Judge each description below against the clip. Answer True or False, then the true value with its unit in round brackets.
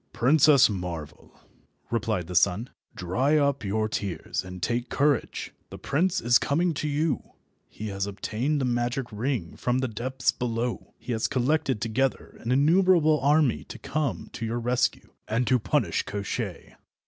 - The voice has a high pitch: False (125 Hz)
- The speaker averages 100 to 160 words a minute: True (155 wpm)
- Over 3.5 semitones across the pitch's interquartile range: True (4.7 semitones)